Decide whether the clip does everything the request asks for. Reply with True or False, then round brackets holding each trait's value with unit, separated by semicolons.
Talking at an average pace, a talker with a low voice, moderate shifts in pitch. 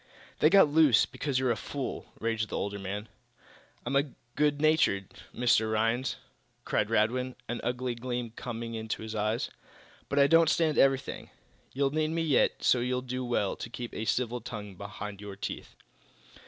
True (170 wpm; 120 Hz; 4.0 semitones)